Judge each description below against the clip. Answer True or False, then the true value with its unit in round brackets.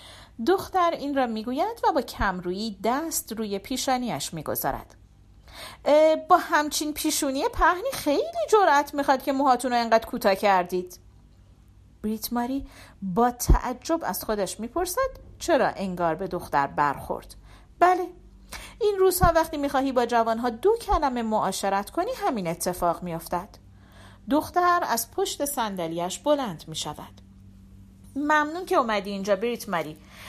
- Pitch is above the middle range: True (235 Hz)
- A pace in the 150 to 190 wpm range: False (120 wpm)